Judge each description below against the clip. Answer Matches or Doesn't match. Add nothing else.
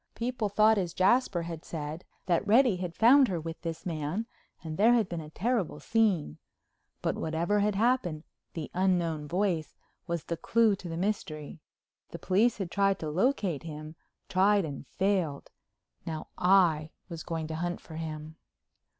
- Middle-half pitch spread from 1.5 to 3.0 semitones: Doesn't match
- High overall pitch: Doesn't match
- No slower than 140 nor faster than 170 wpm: Matches